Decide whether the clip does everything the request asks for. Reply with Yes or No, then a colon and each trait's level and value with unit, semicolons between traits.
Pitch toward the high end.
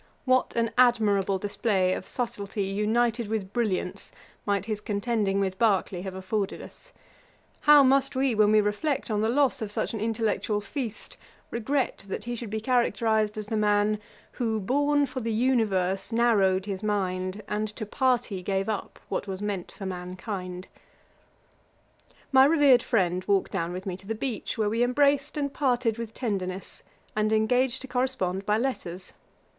Yes: high, 215 Hz